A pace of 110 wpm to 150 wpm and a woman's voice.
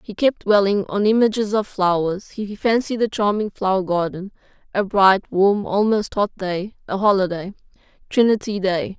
Yes: average, 145 wpm; female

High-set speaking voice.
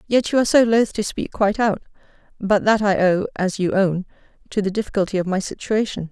Yes: high, 200 Hz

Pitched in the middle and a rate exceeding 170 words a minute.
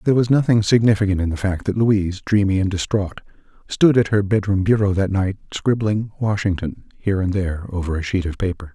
No: low, 100 Hz; average, 200 wpm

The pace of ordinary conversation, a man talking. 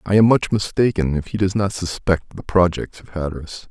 No: fast, 210 wpm; male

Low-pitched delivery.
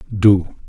Yes: very low, 95 Hz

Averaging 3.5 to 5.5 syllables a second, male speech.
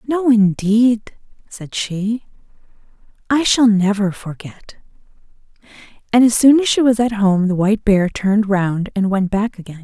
No: 4.4 syllables/s; female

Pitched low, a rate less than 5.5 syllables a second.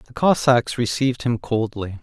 Yes: low, 115 Hz; 4.6 syllables/s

